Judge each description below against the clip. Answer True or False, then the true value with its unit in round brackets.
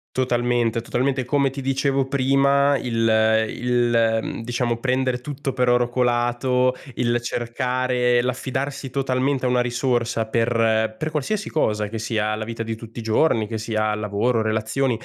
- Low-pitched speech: True (120 Hz)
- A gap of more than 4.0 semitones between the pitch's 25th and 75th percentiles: False (2.4 semitones)